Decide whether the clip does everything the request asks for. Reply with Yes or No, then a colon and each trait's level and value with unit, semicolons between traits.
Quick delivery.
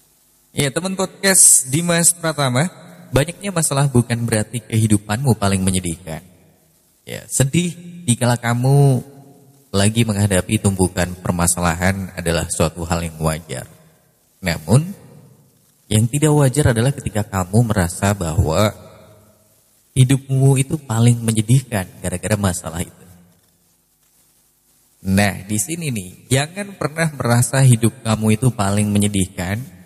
No: average, 105 wpm